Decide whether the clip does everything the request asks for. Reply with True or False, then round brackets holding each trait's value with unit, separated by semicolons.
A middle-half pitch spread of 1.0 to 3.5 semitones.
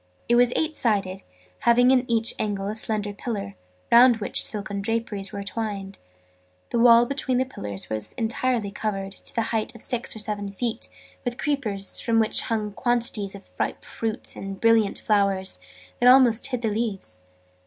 True (3.1 semitones)